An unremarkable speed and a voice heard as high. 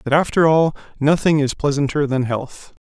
No: average, 170 wpm; medium, 145 Hz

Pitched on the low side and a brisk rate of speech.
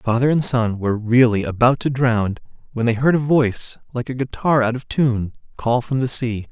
Yes: low, 120 Hz; fast, 210 wpm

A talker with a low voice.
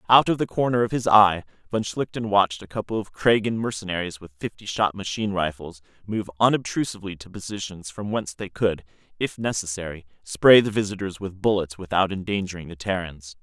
Yes: low, 100 Hz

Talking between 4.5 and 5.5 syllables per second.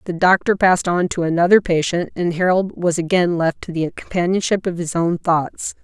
Yes: 5.2 syllables/s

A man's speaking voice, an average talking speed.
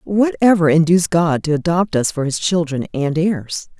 No: female; average, 190 wpm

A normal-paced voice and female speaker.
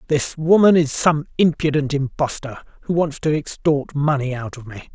No: average, 170 wpm; male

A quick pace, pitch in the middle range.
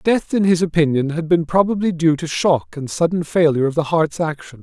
Yes: fast, 220 wpm; medium, 160 Hz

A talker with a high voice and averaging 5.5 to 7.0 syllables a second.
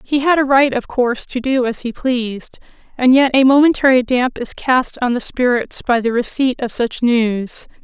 No: very high, 250 Hz; 4.8 syllables/s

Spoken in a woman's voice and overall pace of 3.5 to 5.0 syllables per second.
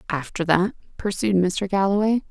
Yes: female; 4.8 syllables/s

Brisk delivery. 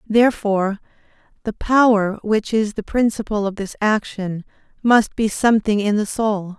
No: average, 145 wpm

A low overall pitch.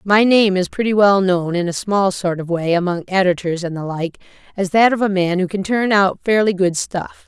No: high, 190 Hz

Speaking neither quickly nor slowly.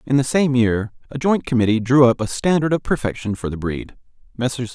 No: fast, 215 wpm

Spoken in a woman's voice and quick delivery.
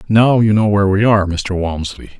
No: male; fast, 220 wpm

